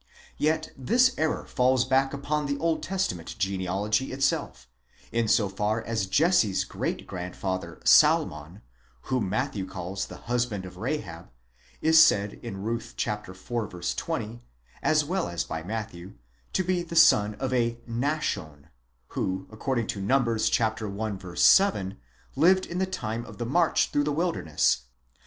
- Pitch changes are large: Yes, wide, 6.8 semitones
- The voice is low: Yes, low, 115 Hz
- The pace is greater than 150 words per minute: No, average, 140 wpm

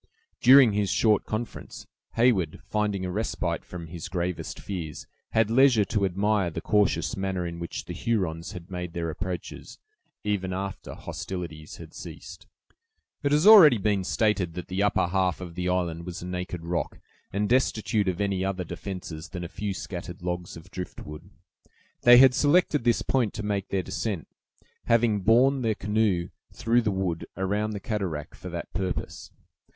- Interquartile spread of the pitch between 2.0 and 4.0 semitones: Yes, average, 3.5 semitones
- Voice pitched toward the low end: Yes, very low, 95 Hz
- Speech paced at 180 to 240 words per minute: No, average, 165 wpm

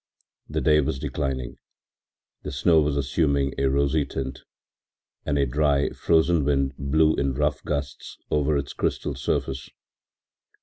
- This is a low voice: Yes, very low, 70 Hz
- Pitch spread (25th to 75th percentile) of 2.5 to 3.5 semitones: No, narrow, 1.8 semitones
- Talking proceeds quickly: No, slow, 135 wpm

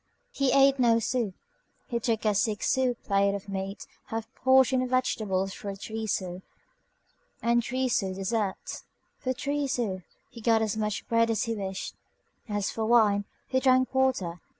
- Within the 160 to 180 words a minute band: Yes, average, 175 wpm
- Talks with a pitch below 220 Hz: No, high, 225 Hz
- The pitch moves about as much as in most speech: Yes, average, 4.2 semitones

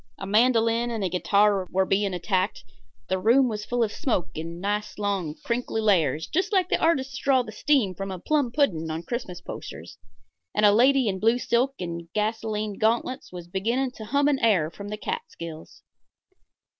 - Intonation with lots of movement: No, average, 4.7 semitones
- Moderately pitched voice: No, high, 210 Hz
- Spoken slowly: No, average, 185 wpm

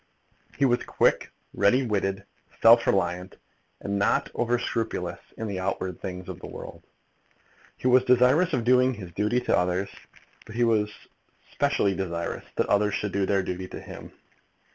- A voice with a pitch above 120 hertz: No, low, 100 Hz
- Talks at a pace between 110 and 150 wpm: No, average, 165 wpm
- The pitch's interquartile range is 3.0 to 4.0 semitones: No, average, 4.6 semitones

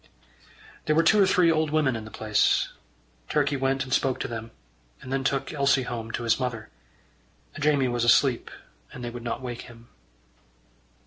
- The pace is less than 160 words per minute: No, average, 180 wpm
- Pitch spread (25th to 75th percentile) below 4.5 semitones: Yes, average, 3.4 semitones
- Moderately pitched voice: No, low, 130 Hz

